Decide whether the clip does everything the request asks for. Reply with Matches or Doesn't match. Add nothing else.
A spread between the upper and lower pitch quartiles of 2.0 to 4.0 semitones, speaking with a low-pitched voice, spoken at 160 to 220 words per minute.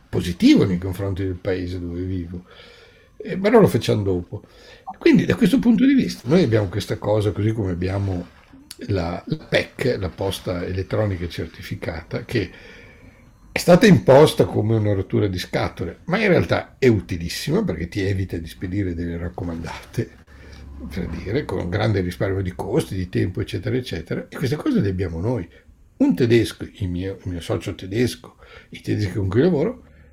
Matches